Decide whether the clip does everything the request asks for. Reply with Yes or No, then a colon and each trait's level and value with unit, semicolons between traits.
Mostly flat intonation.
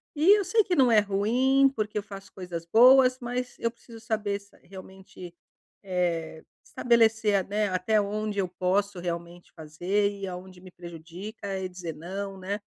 No: average, 3.6 semitones